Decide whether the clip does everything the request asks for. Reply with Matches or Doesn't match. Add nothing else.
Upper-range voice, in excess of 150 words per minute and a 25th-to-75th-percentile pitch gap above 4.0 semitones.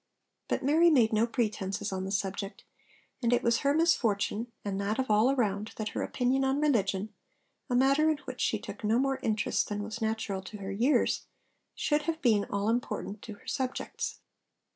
Matches